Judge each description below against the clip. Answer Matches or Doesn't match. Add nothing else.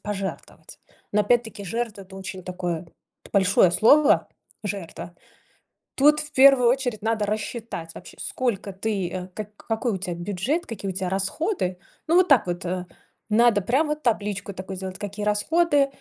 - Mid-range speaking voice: Doesn't match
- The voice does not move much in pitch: Doesn't match